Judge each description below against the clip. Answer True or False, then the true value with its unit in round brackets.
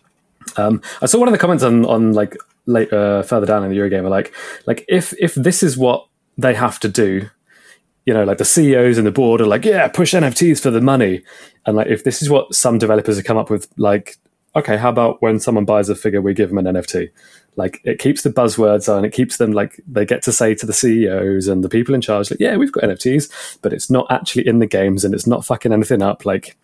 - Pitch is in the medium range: False (110 Hz)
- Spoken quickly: True (250 wpm)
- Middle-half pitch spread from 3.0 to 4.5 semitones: True (3.6 semitones)